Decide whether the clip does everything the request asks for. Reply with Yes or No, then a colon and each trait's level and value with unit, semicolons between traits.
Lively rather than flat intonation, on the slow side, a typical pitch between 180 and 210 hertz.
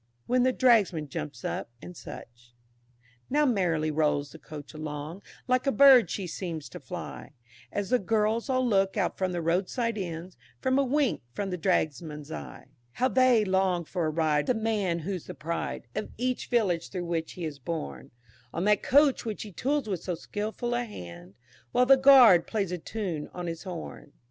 No: wide, 6.6 semitones; average, 190 wpm; high, 190 Hz